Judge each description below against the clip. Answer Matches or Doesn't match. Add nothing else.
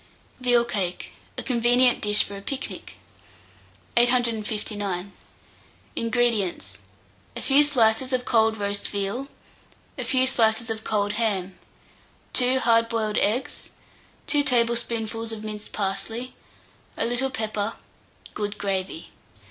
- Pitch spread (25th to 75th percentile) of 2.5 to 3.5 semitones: Matches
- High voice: Matches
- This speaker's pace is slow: Matches